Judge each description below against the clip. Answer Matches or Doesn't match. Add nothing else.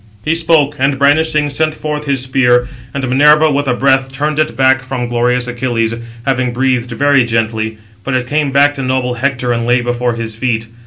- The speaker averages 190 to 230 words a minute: Matches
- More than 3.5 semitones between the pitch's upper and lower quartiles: Doesn't match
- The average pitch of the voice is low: Matches